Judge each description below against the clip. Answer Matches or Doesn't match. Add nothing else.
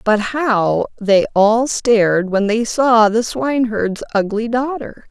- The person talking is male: Doesn't match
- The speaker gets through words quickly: Doesn't match